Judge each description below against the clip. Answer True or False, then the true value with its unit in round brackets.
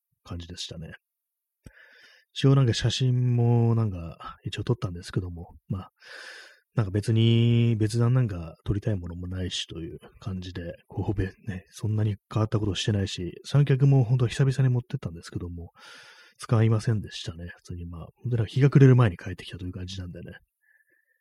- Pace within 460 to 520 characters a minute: False (375 characters per minute)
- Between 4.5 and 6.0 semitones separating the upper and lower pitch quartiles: True (5.5 semitones)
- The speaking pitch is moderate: False (110 Hz)